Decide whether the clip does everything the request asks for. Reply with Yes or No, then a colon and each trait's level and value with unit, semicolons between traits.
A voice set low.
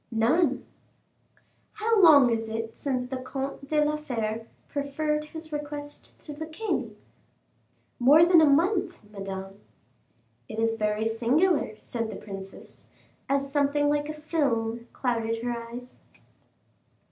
No: very high, 275 Hz